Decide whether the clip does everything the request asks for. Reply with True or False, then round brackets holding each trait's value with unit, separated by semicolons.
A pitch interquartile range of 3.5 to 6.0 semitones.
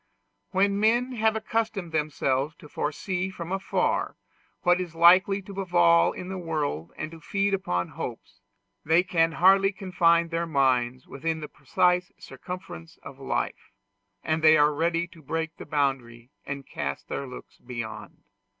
True (5.0 semitones)